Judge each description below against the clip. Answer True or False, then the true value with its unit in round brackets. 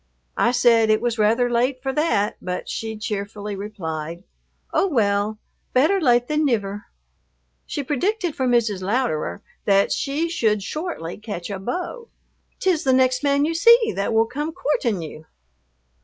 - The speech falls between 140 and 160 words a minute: True (155 wpm)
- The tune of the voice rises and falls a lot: True (6.1 semitones)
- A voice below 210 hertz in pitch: False (235 Hz)